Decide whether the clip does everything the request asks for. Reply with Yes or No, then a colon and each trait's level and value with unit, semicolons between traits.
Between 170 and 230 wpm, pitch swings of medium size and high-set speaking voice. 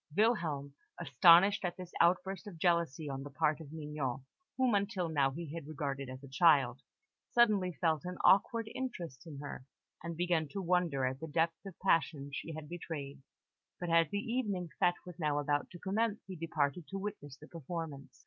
No: average, 185 wpm; average, 4.2 semitones; medium, 165 Hz